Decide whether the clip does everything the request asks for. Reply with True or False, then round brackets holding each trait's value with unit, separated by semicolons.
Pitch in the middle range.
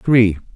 False (110 Hz)